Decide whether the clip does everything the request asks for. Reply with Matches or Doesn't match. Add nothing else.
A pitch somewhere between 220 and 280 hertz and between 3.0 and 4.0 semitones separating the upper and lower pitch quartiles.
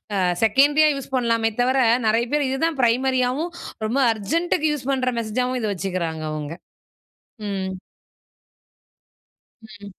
Doesn't match